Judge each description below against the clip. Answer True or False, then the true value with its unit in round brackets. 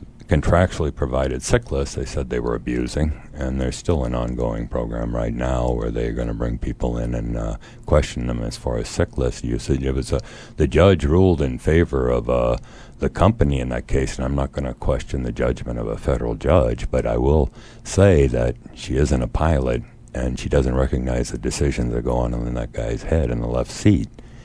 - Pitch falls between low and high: False (65 Hz)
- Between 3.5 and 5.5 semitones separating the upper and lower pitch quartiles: True (3.9 semitones)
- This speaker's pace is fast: True (215 wpm)